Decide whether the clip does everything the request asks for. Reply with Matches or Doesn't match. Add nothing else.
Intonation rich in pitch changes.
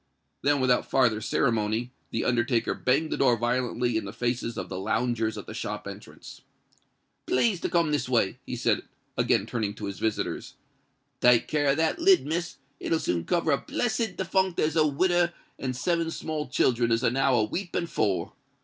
Matches